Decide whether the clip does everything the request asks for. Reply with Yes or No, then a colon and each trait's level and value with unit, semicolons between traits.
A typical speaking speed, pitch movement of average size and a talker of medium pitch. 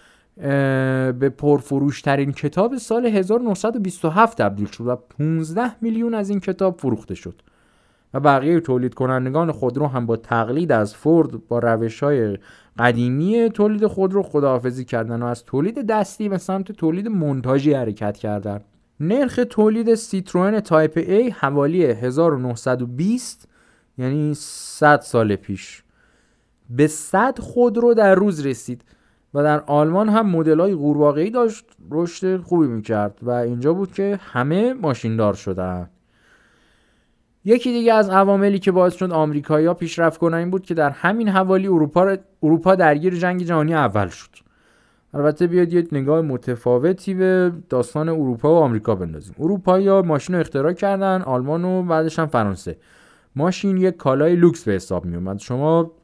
No: average, 140 wpm; wide, 7.2 semitones; medium, 155 Hz